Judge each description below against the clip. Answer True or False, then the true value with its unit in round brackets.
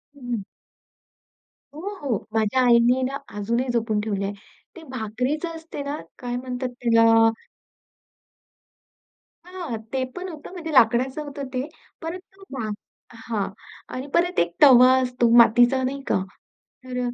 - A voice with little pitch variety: False (3.8 semitones)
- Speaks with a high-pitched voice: True (255 Hz)